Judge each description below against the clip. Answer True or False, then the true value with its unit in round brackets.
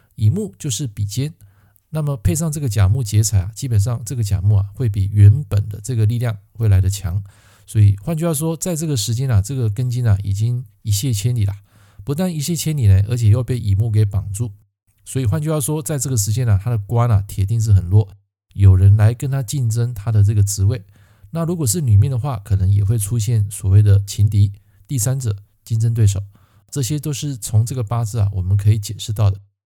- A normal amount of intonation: True (3.7 semitones)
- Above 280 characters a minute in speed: True (320 characters per minute)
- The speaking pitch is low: True (110 Hz)